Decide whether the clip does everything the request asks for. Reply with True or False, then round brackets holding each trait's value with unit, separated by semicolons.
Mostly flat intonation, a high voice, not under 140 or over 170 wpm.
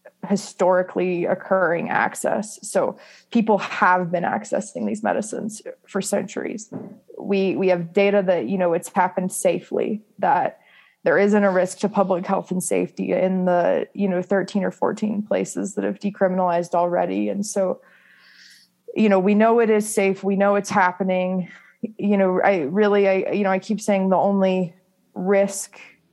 True (1.7 semitones; 195 Hz; 160 wpm)